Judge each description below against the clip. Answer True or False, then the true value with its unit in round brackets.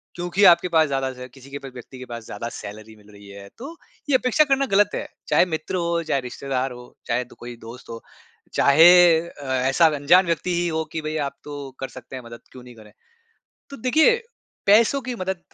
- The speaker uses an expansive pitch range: True (6.3 semitones)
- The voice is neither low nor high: True (145 Hz)